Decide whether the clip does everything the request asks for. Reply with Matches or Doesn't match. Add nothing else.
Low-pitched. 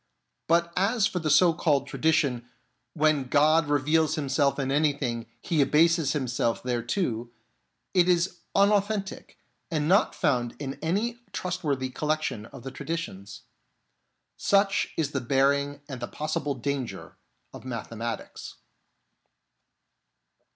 Doesn't match